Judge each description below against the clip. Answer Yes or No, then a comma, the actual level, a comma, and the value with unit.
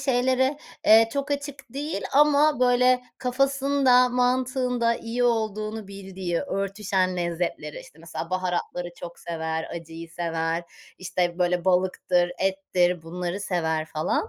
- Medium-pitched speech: No, high, 195 Hz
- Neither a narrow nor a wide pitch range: No, wide, 6.3 semitones